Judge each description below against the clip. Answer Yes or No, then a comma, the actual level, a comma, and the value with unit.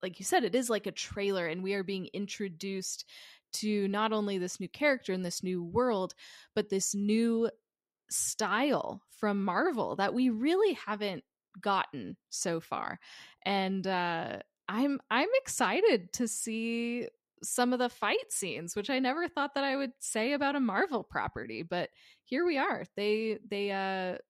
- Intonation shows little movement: No, average, 4.7 semitones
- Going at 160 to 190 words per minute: Yes, average, 165 wpm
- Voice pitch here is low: No, high, 215 Hz